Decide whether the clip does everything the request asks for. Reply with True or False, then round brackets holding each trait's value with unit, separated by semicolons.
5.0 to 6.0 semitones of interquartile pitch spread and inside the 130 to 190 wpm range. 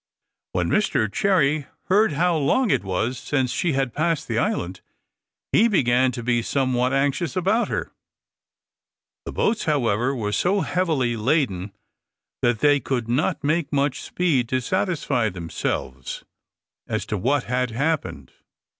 True (5.5 semitones; 140 wpm)